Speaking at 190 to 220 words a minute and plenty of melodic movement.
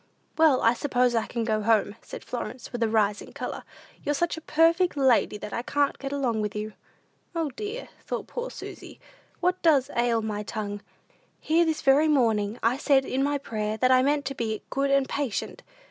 No: average, 195 wpm; average, 4.8 semitones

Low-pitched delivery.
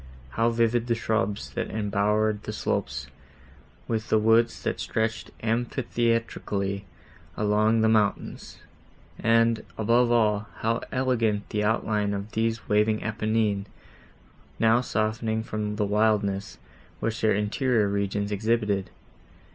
Yes: low, 110 Hz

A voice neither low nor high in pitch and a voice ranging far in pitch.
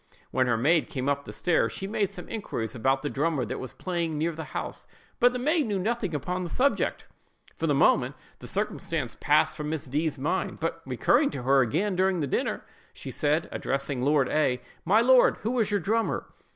Yes: medium, 160 Hz; wide, 6.5 semitones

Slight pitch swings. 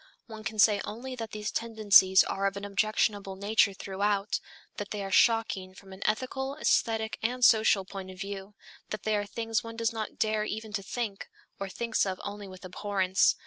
Yes: narrow, 2.2 semitones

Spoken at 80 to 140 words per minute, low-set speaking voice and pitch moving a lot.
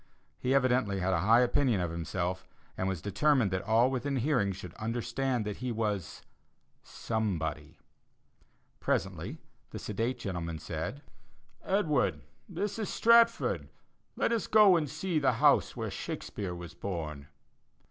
Yes: slow, 135 wpm; low, 115 Hz; wide, 6.7 semitones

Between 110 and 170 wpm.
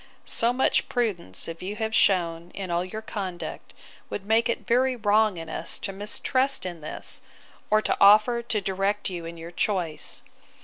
No: average, 180 wpm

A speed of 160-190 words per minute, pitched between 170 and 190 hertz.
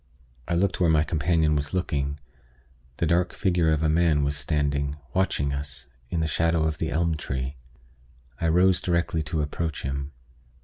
No: average, 170 wpm; very low, 80 Hz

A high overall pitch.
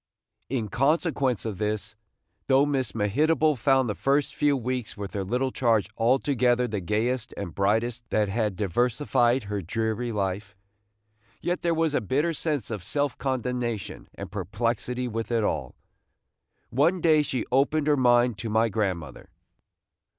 No: low, 120 Hz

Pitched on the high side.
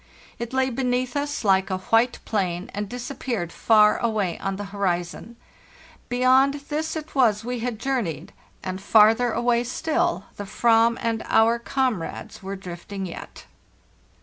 Yes: high, 230 Hz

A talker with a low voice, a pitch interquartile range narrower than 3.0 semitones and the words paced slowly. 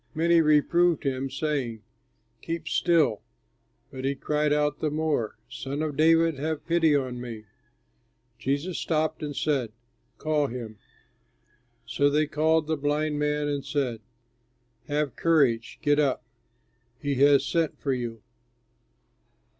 No: medium, 145 Hz; narrow, 2.6 semitones; slow, 130 wpm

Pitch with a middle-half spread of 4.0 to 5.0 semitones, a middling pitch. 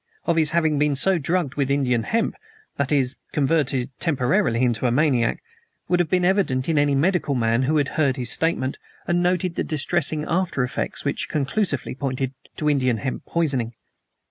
Yes: average, 4.4 semitones; medium, 145 Hz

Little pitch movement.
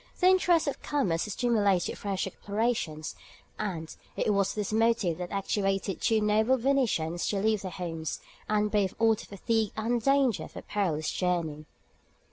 No: average, 4.1 semitones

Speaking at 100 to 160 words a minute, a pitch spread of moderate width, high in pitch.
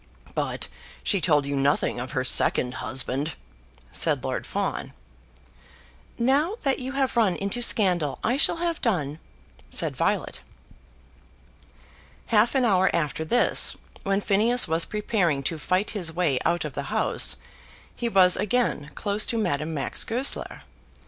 No: average, 140 wpm; wide, 7.5 semitones; high, 195 Hz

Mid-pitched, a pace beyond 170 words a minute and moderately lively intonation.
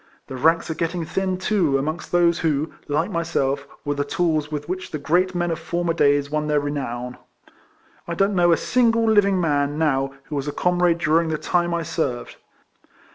Yes: medium, 160 Hz; average, 190 wpm; average, 3.4 semitones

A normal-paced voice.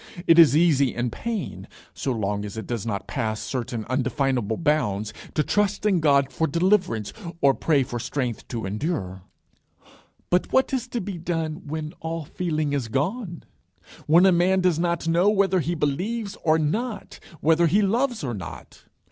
Yes: average, 170 wpm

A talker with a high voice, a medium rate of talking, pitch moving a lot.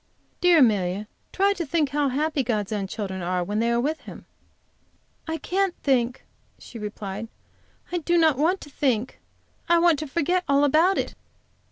Yes: very high, 280 Hz; average, 175 wpm; wide, 7.6 semitones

